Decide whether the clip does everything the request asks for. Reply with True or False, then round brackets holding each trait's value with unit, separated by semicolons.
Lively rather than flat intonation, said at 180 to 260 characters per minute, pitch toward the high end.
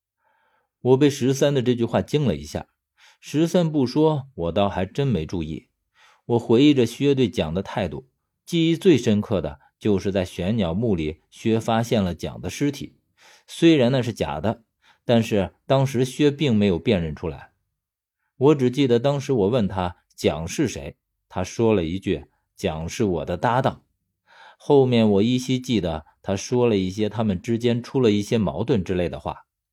False (5.8 semitones; 245 characters per minute; 115 Hz)